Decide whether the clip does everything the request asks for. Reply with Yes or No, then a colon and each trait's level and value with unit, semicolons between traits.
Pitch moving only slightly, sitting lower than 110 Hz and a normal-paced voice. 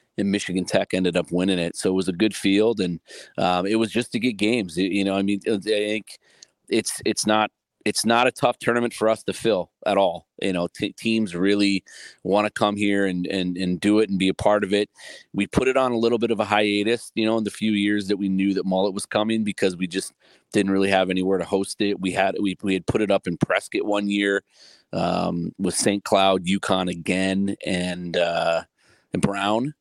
No: narrow, 2.2 semitones; low, 100 Hz; fast, 230 wpm